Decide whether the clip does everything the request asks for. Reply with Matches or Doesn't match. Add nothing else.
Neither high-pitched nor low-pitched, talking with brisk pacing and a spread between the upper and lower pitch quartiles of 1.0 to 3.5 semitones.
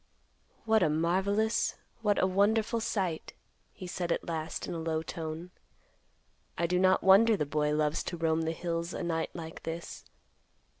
Doesn't match